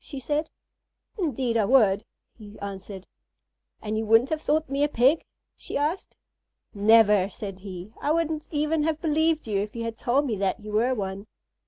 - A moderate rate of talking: Yes, average, 180 wpm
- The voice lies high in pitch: Yes, high, 230 Hz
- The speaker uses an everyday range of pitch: No, wide, 6.4 semitones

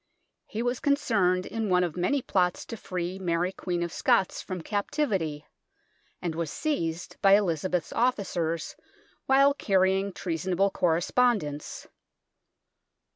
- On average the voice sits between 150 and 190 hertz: Yes, medium, 185 Hz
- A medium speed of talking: No, slow, 125 wpm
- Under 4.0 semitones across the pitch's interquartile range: No, average, 4.3 semitones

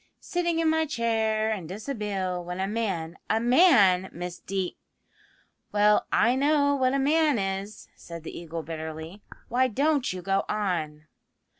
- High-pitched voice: Yes, high, 210 Hz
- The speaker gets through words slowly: No, average, 155 wpm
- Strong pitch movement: Yes, wide, 6.5 semitones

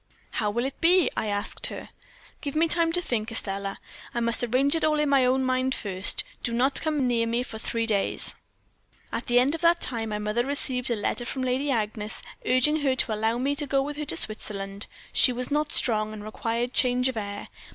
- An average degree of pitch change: Yes, average, 4.2 semitones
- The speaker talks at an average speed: No, fast, 220 wpm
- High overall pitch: Yes, high, 245 Hz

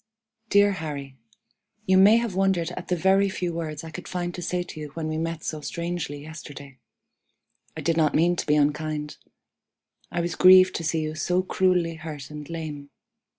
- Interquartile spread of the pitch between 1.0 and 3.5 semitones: Yes, average, 2.9 semitones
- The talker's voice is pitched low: No, medium, 165 Hz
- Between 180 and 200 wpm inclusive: Yes, average, 190 wpm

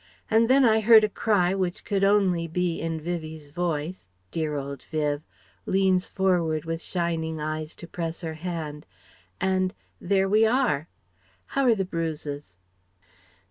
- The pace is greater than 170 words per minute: No, average, 140 wpm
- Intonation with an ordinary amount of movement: Yes, average, 3.5 semitones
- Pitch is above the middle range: No, medium, 170 Hz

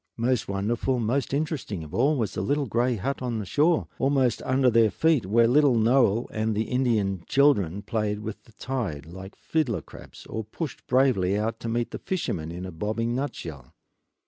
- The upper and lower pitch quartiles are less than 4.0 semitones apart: No, average, 4.5 semitones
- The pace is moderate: Yes, average, 185 wpm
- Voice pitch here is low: Yes, low, 115 Hz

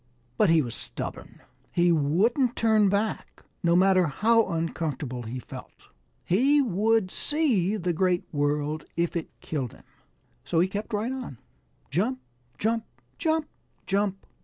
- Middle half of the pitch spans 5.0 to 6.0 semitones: Yes, wide, 5.6 semitones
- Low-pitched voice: No, high, 190 Hz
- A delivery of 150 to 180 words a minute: No, slow, 135 wpm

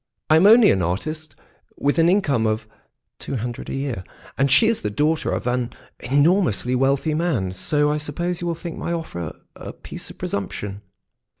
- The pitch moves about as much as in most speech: No, wide, 6.1 semitones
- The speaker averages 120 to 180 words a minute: No, average, 190 wpm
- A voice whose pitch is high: No, medium, 145 Hz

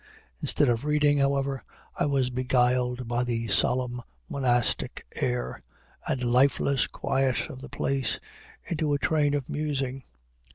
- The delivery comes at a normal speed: No, slow, 130 wpm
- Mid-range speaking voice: No, low, 130 Hz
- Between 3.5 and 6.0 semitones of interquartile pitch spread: No, narrow, 2.4 semitones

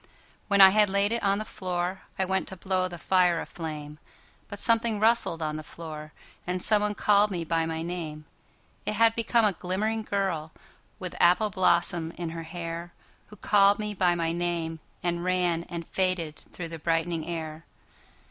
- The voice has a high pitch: No, medium, 180 Hz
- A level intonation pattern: No, average, 3.3 semitones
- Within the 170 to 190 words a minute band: No, average, 155 wpm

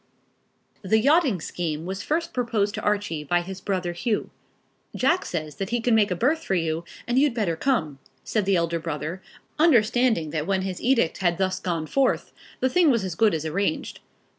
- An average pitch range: No, wide, 6.1 semitones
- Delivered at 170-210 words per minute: Yes, average, 190 wpm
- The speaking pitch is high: Yes, high, 195 Hz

